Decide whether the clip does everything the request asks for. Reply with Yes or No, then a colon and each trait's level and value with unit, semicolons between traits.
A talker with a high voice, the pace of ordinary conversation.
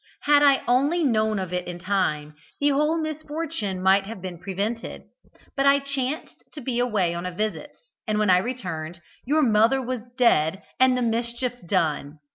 Yes: high, 225 Hz; average, 175 wpm